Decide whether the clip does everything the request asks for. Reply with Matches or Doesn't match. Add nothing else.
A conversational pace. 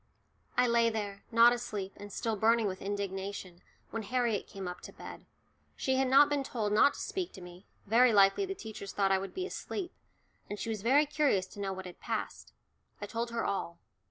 Doesn't match